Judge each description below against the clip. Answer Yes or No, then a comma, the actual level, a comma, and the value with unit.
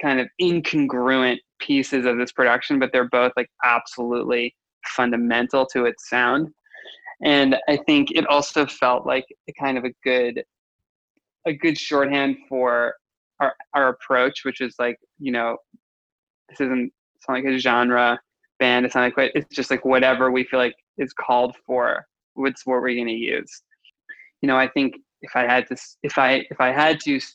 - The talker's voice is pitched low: Yes, low, 130 Hz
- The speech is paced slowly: No, average, 180 wpm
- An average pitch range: No, narrow, 2.2 semitones